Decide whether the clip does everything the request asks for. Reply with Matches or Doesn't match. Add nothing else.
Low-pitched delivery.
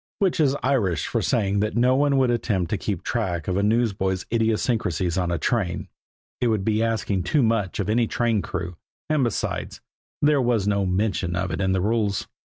Matches